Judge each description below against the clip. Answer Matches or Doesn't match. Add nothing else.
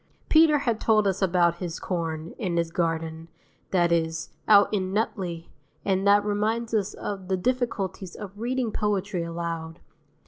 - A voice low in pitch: Doesn't match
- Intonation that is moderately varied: Matches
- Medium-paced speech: Matches